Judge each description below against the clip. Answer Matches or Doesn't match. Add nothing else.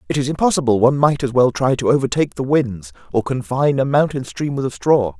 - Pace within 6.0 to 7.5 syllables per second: Matches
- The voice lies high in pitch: Doesn't match